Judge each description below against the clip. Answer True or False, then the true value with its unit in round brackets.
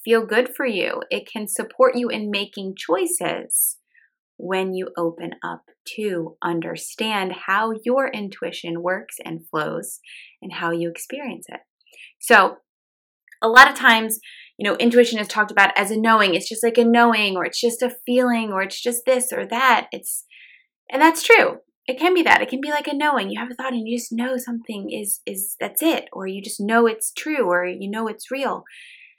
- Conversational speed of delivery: True (195 wpm)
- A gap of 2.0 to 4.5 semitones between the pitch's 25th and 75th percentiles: False (5.1 semitones)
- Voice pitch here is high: True (230 Hz)